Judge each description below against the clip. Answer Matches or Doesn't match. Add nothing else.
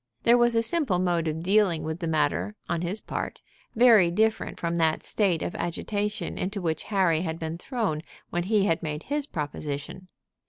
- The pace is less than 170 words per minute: Doesn't match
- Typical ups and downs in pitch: Matches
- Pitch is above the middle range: Doesn't match